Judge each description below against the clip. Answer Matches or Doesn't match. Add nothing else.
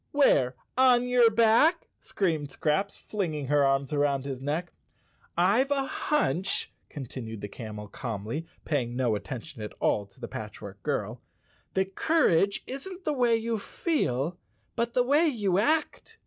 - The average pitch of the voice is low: Doesn't match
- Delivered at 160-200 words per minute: Doesn't match